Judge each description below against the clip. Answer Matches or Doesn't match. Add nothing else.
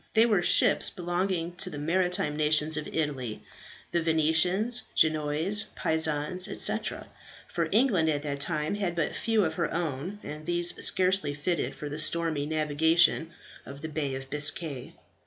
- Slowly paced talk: Doesn't match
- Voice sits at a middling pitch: Matches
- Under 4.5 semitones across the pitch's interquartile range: Matches